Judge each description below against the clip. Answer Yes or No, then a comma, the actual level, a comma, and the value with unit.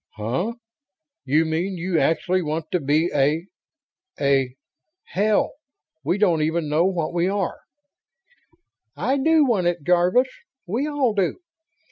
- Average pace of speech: No, slow, 130 wpm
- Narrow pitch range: No, average, 4.4 semitones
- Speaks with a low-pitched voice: No, medium, 175 Hz